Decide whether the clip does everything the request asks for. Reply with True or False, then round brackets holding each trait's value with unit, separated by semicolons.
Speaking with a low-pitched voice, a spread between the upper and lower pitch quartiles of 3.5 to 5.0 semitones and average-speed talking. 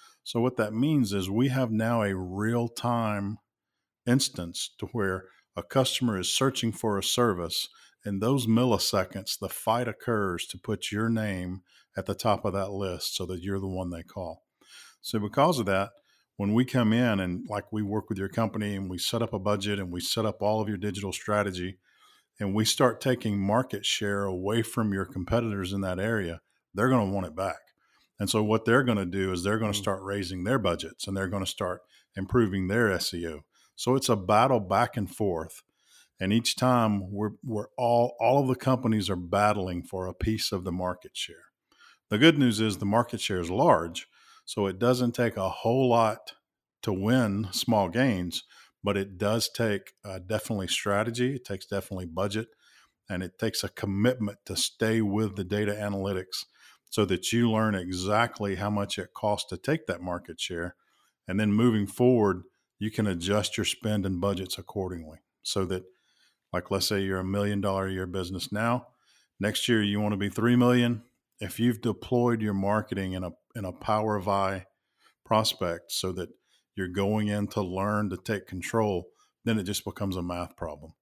False (105 Hz; 3.0 semitones; 195 wpm)